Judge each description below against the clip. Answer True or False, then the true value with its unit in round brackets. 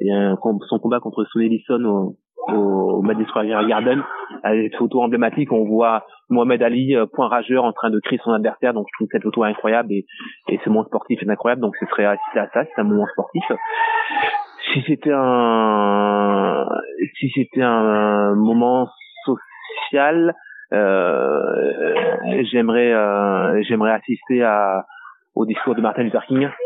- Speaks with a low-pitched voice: True (120 Hz)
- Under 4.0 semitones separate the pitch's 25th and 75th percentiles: False (5.1 semitones)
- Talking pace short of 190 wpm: True (155 wpm)